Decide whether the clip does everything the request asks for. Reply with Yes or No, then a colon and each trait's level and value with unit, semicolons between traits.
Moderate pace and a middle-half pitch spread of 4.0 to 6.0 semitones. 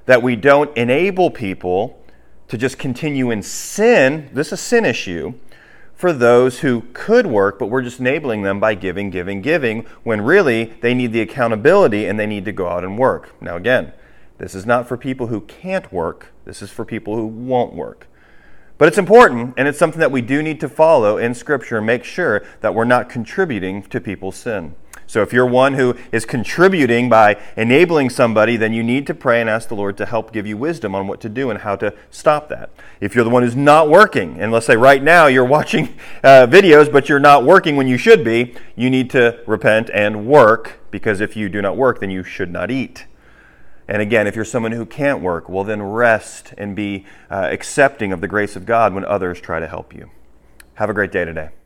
No: fast, 220 wpm; average, 4.5 semitones